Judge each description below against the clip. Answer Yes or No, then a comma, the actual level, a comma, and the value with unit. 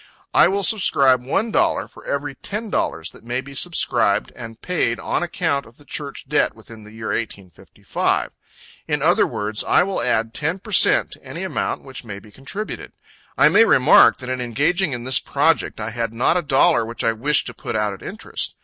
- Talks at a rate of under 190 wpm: No, fast, 205 wpm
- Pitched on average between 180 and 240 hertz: No, low, 130 Hz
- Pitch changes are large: Yes, wide, 6.3 semitones